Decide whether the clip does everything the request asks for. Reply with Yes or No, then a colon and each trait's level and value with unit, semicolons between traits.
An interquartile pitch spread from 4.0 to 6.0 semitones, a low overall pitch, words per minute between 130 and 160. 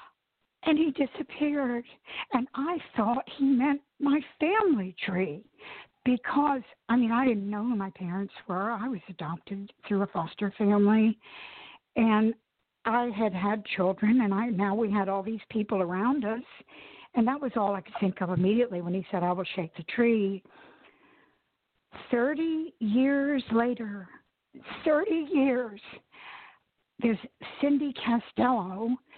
No: average, 4.7 semitones; high, 230 Hz; average, 140 wpm